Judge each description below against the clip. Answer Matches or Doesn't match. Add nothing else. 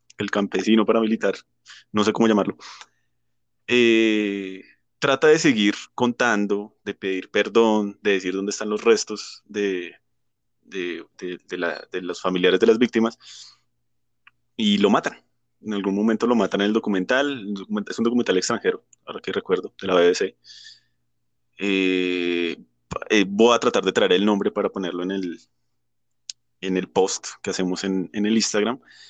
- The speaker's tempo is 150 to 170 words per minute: Matches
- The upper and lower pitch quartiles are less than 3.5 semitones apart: Doesn't match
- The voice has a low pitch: Matches